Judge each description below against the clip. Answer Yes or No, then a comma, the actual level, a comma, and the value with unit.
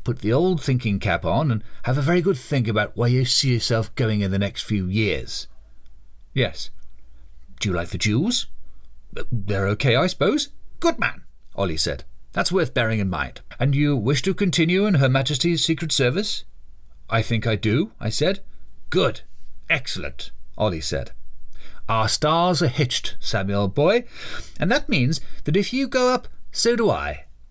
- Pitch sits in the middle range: No, low, 120 Hz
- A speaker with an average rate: Yes, average, 170 wpm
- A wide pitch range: Yes, wide, 8.2 semitones